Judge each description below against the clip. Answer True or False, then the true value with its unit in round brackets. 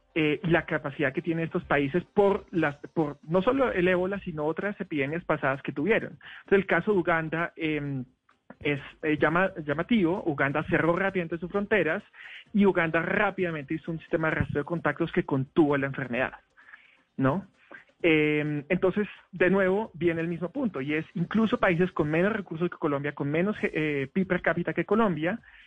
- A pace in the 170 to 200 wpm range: True (175 wpm)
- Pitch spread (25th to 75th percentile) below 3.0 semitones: False (3.6 semitones)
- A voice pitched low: False (170 Hz)